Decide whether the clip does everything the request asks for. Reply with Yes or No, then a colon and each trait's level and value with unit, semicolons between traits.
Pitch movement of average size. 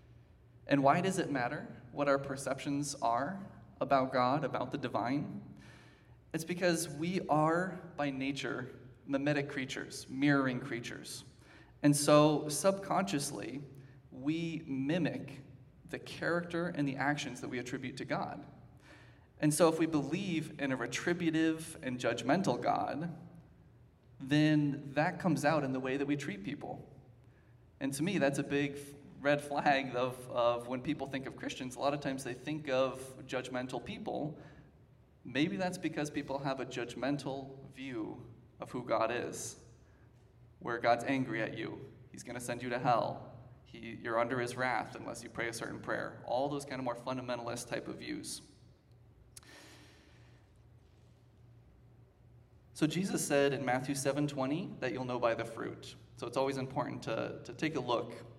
Yes: average, 3.0 semitones